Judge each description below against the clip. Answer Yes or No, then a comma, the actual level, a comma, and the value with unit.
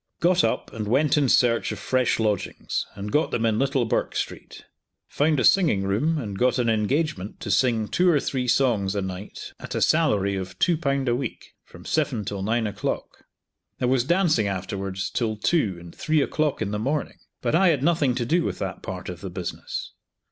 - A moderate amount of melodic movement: No, wide, 6.8 semitones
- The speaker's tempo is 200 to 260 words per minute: Yes, fast, 205 wpm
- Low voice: Yes, low, 120 Hz